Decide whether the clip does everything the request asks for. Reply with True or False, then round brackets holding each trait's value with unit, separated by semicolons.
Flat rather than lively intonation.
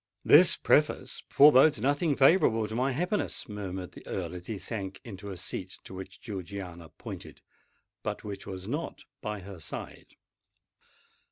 False (5.6 semitones)